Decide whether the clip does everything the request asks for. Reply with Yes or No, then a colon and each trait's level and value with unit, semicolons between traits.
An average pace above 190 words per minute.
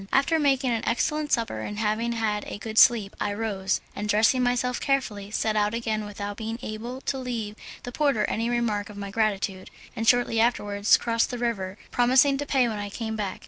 Yes: average, 200 wpm